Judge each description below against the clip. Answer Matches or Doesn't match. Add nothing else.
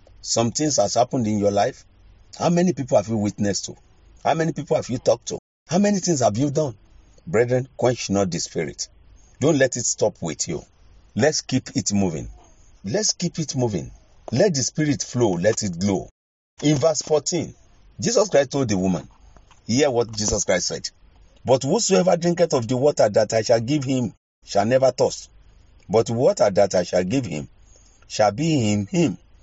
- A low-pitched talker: Matches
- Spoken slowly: Doesn't match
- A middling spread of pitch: Doesn't match